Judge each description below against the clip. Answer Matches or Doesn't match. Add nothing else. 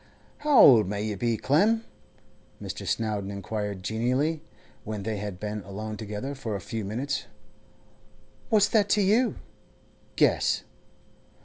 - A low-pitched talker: Matches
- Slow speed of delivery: Matches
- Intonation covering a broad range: Matches